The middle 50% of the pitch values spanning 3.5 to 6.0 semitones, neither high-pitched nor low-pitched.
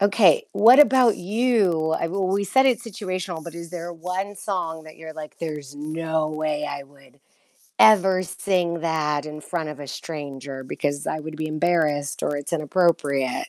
Yes: average, 3.8 semitones; medium, 160 Hz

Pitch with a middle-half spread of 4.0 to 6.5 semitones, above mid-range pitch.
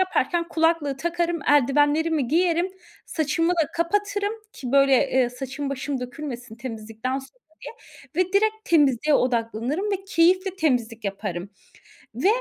Yes: wide, 5.4 semitones; very high, 290 Hz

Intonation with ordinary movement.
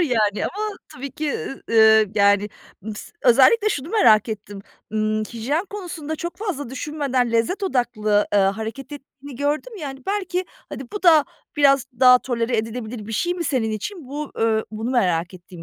No: wide, 5.7 semitones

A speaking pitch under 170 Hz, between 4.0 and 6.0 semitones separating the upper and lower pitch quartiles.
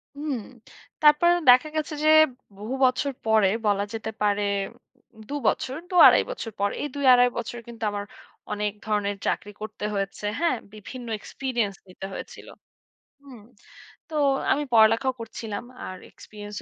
No: high, 225 Hz; average, 4.6 semitones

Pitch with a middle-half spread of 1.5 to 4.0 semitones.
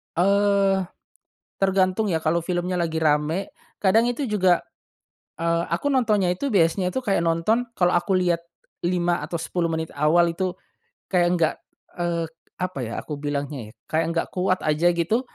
Yes: average, 2.7 semitones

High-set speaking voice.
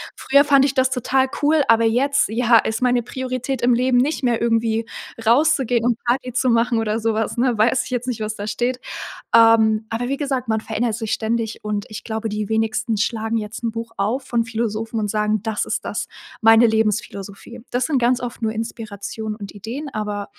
Yes: high, 230 Hz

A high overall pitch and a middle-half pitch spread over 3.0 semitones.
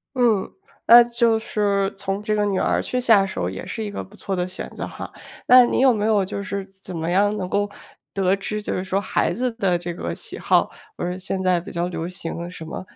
No: high, 195 Hz; narrow, 2.6 semitones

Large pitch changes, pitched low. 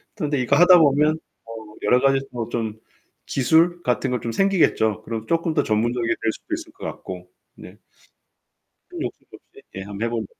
Yes: wide, 6.5 semitones; low, 125 Hz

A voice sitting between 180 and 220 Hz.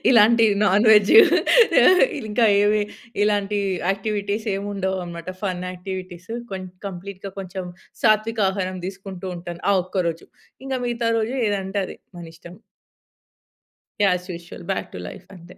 Yes: high, 195 Hz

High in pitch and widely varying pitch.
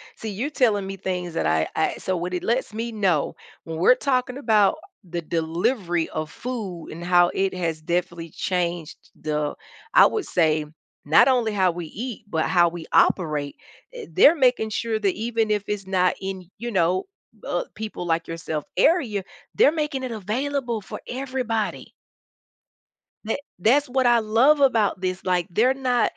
Yes: high, 195 Hz; wide, 5.8 semitones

